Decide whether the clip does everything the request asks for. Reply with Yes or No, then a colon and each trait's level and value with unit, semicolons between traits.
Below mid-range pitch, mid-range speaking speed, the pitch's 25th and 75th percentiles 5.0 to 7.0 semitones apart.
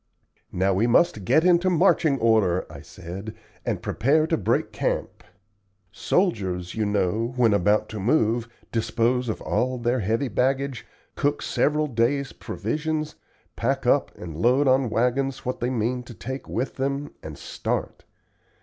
No: low, 120 Hz; average, 150 wpm; average, 4.4 semitones